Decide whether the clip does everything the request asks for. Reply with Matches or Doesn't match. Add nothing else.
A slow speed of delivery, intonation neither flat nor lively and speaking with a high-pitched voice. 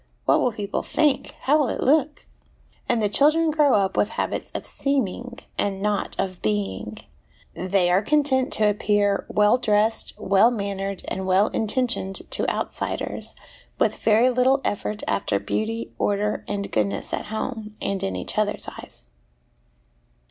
Doesn't match